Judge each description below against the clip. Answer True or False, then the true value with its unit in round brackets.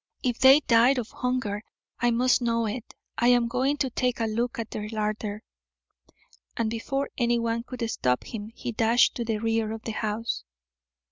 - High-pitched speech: True (230 Hz)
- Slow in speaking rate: False (180 wpm)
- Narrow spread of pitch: True (2.0 semitones)